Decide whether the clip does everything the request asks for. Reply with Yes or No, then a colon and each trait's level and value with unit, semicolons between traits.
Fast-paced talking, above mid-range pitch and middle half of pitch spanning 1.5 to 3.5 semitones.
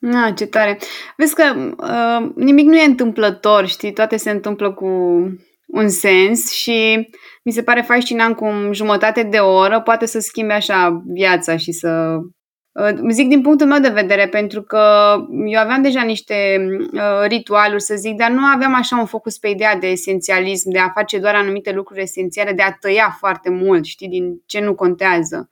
Yes: fast, 185 wpm; high, 210 Hz; average, 3.1 semitones